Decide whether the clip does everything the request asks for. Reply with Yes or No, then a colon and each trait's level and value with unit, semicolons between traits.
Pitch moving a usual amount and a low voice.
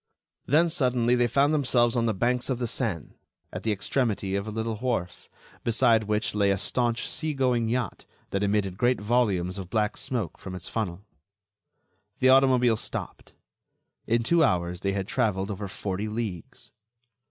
Yes: average, 4.0 semitones; low, 110 Hz